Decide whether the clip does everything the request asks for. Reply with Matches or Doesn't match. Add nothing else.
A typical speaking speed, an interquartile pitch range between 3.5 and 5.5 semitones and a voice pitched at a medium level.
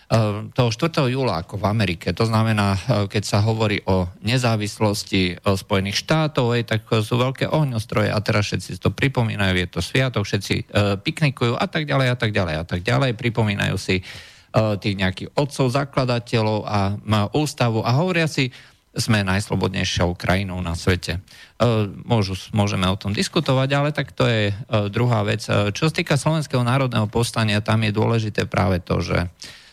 Doesn't match